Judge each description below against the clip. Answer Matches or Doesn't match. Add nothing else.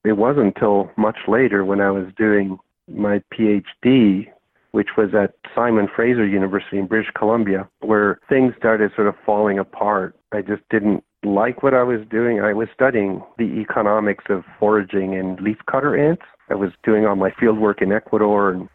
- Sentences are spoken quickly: Doesn't match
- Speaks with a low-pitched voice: Matches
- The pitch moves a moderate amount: Doesn't match